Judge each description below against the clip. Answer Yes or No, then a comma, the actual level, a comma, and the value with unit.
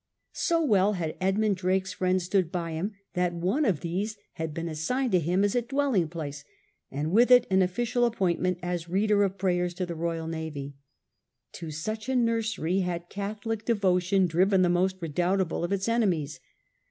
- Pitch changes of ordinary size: Yes, average, 3.6 semitones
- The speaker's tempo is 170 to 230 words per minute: Yes, average, 175 wpm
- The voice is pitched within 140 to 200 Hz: Yes, medium, 185 Hz